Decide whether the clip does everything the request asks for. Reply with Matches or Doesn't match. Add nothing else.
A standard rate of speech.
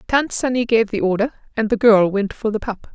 Doesn't match